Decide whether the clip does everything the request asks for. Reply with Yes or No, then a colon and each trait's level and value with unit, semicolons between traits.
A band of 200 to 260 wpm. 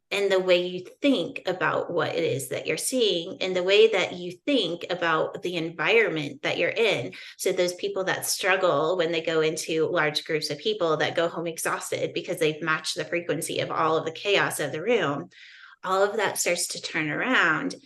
Yes: fast, 205 wpm